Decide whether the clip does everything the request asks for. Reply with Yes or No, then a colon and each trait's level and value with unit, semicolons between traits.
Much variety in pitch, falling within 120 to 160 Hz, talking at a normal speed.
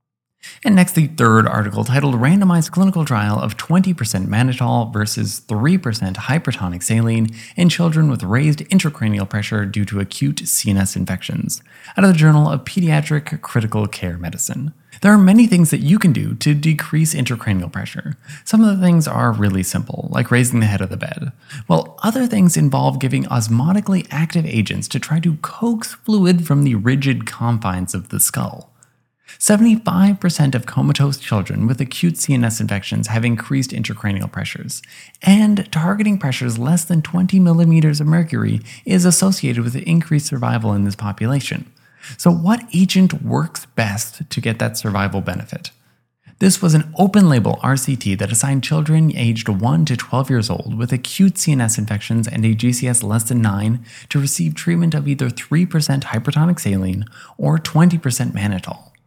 Yes: wide, 6.8 semitones; low, 135 Hz; average, 160 wpm